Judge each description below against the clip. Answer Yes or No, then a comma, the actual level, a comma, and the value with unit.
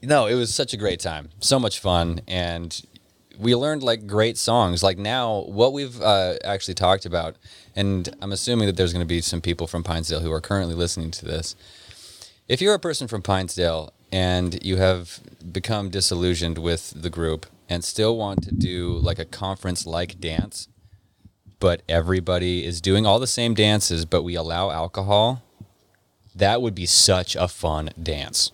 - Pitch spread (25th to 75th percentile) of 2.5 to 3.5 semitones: Yes, average, 3.2 semitones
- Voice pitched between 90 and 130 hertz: Yes, very low, 95 Hz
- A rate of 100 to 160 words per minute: No, average, 175 wpm